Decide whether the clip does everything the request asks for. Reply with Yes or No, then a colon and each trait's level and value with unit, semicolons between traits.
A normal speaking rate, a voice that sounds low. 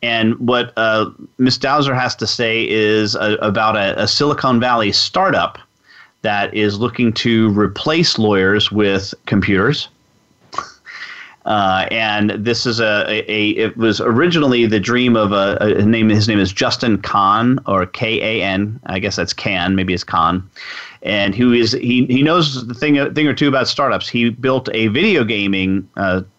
Yes: average, 165 wpm; low, 110 Hz